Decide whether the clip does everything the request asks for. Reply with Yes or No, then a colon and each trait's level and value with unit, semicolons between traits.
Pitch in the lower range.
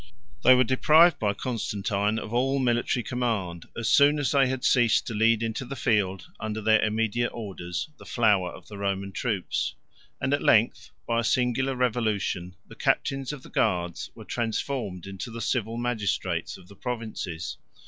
Yes: low, 115 Hz